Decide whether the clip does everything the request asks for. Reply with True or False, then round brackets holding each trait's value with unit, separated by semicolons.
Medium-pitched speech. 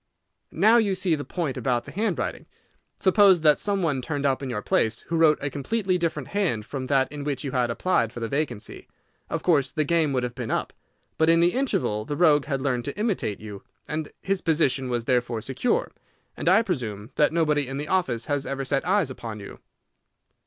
True (145 Hz)